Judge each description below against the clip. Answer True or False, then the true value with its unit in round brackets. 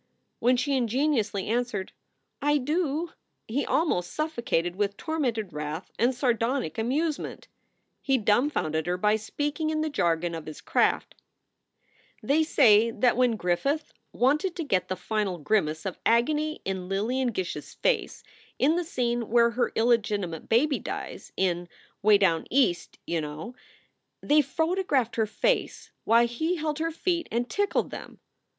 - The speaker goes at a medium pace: True (145 wpm)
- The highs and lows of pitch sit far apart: True (7.3 semitones)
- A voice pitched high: True (235 Hz)